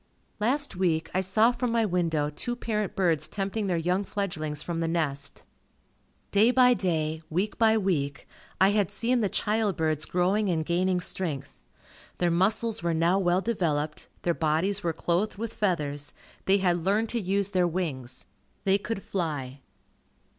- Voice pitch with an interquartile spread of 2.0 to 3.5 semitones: No, average, 4.3 semitones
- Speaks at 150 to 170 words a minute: Yes, average, 160 wpm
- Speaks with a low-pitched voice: No, medium, 185 Hz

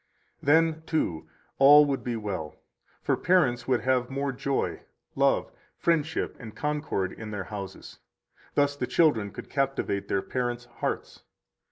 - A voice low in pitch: Yes, low, 130 Hz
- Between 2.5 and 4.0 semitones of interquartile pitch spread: No, average, 5.3 semitones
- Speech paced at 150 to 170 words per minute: No, average, 140 wpm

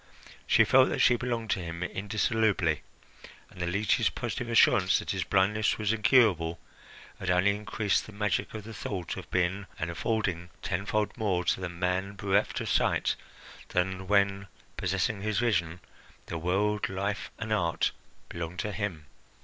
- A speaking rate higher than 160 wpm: No, average, 155 wpm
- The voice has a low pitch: Yes, low, 100 Hz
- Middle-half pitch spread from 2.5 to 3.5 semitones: Yes, average, 3.0 semitones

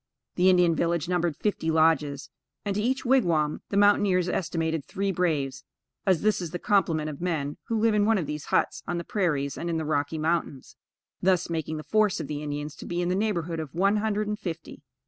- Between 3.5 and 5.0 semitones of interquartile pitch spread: Yes, average, 4.3 semitones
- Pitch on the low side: No, medium, 170 Hz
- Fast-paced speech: Yes, fast, 215 wpm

